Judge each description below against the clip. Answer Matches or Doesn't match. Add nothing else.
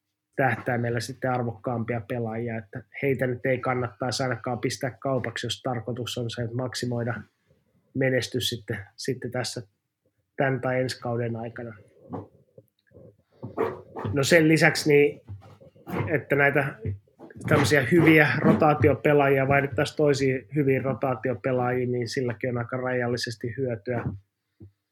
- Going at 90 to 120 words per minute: Matches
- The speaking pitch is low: Matches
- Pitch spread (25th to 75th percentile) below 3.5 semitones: Matches